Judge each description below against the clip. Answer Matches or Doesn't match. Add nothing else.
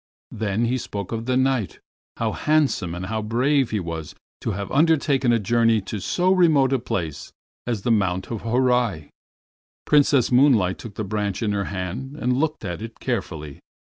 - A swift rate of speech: Doesn't match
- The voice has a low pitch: Matches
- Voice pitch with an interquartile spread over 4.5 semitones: Matches